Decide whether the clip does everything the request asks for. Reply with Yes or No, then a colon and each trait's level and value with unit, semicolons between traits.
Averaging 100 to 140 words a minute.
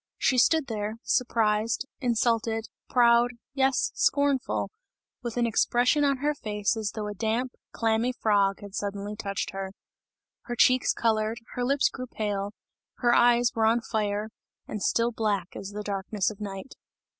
No: average, 155 wpm